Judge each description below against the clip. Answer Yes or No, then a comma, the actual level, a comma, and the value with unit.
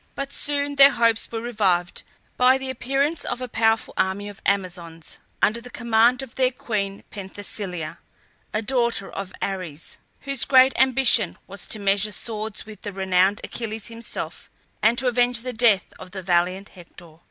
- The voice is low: No, high, 220 Hz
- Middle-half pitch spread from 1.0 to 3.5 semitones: No, average, 4.4 semitones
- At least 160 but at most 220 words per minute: Yes, average, 165 wpm